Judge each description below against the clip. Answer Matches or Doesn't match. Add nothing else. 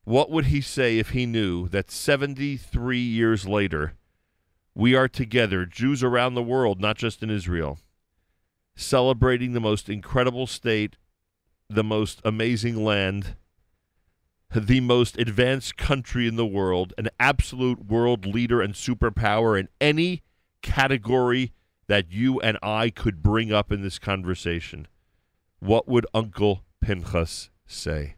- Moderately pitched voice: Doesn't match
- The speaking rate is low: Matches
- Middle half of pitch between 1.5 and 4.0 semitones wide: Doesn't match